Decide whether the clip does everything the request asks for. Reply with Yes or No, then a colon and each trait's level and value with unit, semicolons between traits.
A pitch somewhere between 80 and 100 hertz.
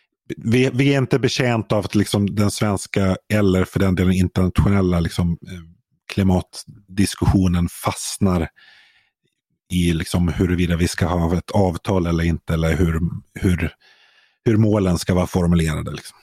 Yes: very low, 95 Hz